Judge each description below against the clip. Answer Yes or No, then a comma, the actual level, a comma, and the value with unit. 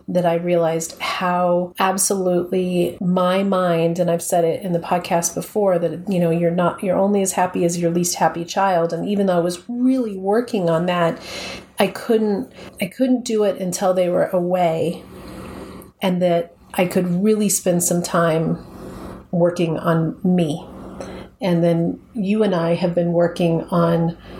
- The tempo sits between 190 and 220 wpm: No, average, 165 wpm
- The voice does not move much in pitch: Yes, narrow, 2.1 semitones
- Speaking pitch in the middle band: Yes, medium, 180 Hz